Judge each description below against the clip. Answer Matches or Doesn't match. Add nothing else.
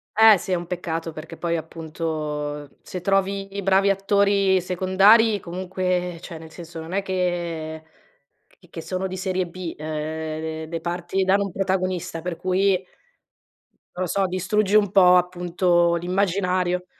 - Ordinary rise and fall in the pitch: Doesn't match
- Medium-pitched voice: Matches